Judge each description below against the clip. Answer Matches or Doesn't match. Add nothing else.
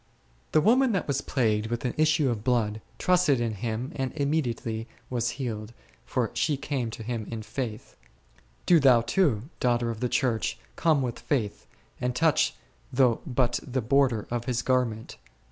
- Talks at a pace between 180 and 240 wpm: Doesn't match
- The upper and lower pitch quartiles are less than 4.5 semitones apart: Matches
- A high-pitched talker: Doesn't match